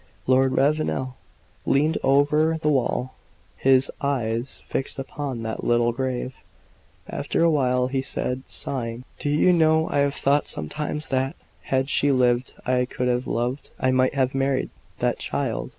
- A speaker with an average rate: Yes, average, 150 wpm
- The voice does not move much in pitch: Yes, narrow, 2.1 semitones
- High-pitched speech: No, low, 130 Hz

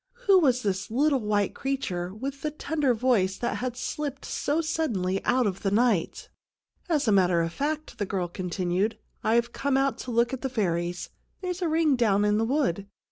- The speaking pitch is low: No, high, 235 Hz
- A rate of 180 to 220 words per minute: Yes, fast, 205 wpm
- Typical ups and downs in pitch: No, wide, 6.2 semitones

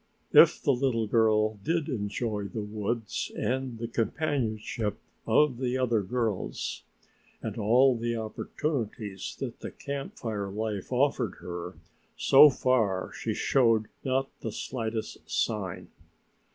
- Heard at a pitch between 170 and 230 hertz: No, low, 115 Hz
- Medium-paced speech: No, slow, 125 wpm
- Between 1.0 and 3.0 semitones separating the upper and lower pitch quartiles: No, average, 3.4 semitones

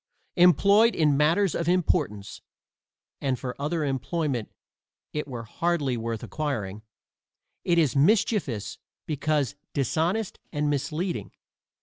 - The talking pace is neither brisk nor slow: No, slow, 105 wpm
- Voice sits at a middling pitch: Yes, medium, 150 Hz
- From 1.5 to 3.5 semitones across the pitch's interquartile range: No, average, 4.9 semitones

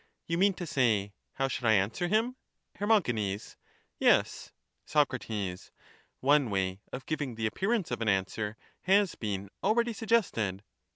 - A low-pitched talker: Yes, low, 130 Hz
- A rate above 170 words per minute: No, slow, 135 wpm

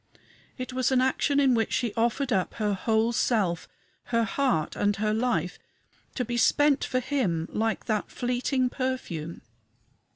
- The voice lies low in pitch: No, high, 235 Hz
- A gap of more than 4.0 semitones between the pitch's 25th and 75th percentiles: No, average, 3.4 semitones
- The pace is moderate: Yes, average, 155 wpm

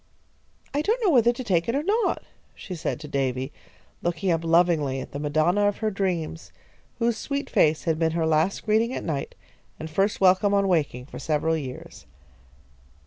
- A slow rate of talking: No, average, 185 wpm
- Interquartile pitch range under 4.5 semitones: No, average, 5.3 semitones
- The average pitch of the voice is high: No, medium, 170 Hz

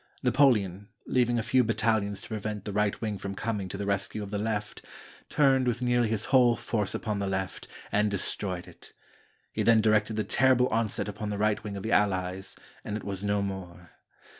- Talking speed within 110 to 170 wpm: No, average, 200 wpm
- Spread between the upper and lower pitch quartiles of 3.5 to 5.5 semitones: No, narrow, 2.4 semitones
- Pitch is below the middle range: Yes, low, 105 Hz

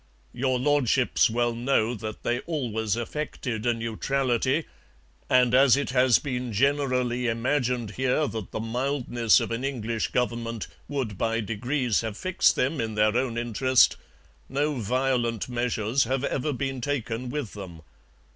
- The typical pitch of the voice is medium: No, low, 125 Hz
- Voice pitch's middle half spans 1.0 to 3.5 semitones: Yes, average, 2.8 semitones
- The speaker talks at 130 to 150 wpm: Yes, average, 145 wpm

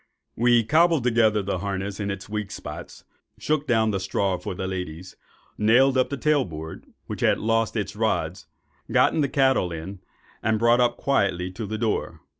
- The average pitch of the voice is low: Yes, low, 110 Hz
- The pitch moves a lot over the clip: No, average, 4.2 semitones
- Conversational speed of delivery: Yes, average, 175 wpm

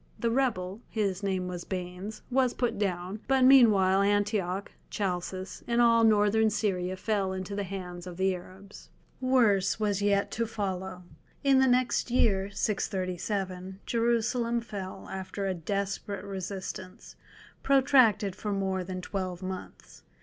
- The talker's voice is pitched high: Yes, high, 200 Hz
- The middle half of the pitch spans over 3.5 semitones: No, average, 3.0 semitones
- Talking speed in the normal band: No, slow, 130 wpm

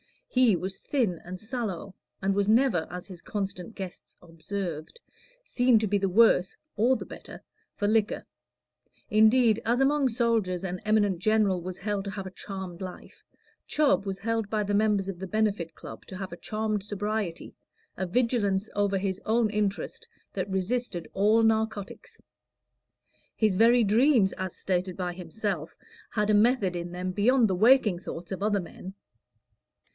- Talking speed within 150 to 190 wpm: Yes, average, 160 wpm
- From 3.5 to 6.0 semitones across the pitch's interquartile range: No, average, 3.0 semitones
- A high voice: Yes, high, 200 Hz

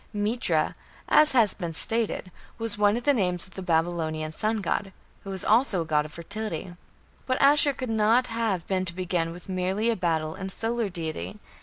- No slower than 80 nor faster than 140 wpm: No, average, 190 wpm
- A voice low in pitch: No, high, 190 Hz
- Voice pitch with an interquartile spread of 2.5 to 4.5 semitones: No, average, 4.9 semitones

